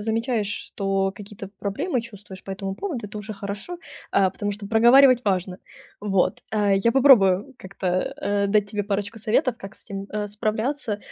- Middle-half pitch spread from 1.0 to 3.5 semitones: Yes, narrow, 2.5 semitones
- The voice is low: No, high, 205 Hz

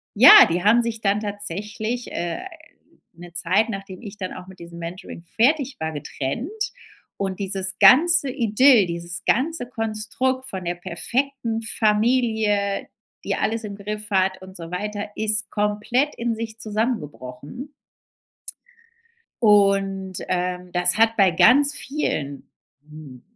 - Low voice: No, high, 210 Hz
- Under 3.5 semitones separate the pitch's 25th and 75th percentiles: No, average, 4.1 semitones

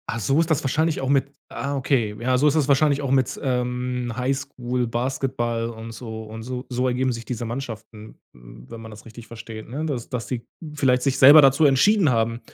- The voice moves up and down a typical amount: Yes, average, 3.0 semitones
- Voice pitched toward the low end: Yes, low, 125 Hz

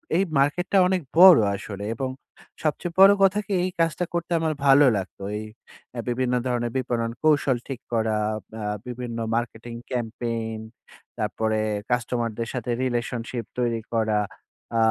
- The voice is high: No, low, 120 Hz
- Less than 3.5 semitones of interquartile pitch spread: No, average, 4.3 semitones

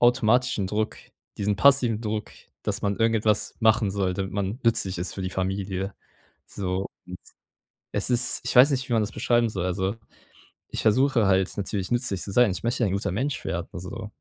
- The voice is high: No, low, 105 Hz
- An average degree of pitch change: Yes, average, 3.7 semitones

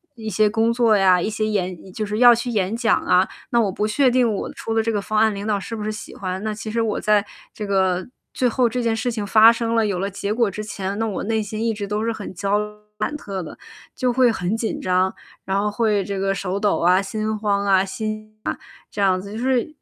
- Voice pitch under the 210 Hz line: No, high, 215 Hz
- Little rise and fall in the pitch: Yes, narrow, 2.2 semitones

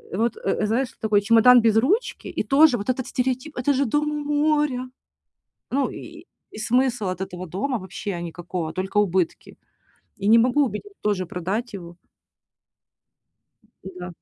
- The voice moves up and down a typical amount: No, wide, 6.0 semitones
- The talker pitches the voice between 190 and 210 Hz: No, high, 230 Hz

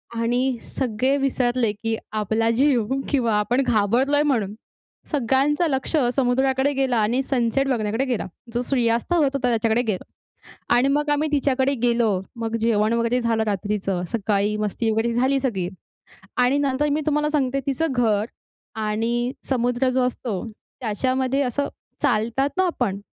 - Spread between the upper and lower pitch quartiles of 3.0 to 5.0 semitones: Yes, average, 3.3 semitones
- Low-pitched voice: No, high, 245 Hz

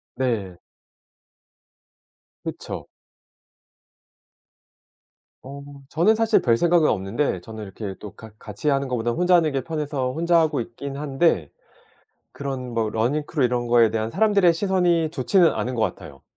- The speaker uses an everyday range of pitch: No, wide, 6.3 semitones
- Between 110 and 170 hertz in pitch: Yes, low, 135 Hz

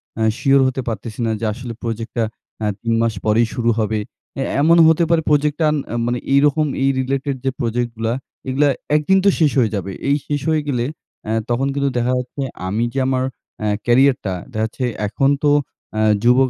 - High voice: No, low, 125 Hz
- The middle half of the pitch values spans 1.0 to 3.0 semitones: No, average, 3.5 semitones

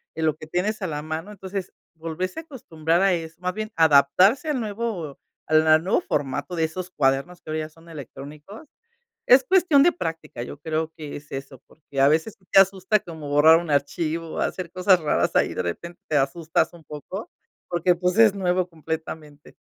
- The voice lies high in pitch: No, medium, 165 Hz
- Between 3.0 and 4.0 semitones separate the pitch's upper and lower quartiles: Yes, average, 3.7 semitones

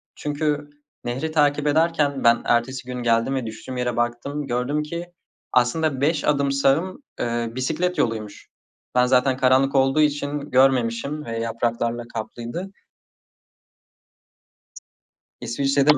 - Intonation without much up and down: No, average, 3.6 semitones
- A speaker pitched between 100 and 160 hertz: Yes, low, 135 Hz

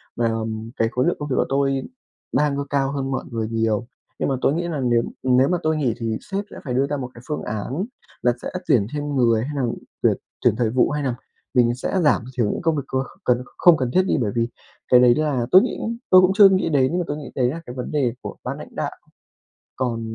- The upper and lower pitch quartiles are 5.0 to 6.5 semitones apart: No, average, 3.8 semitones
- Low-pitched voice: Yes, low, 130 Hz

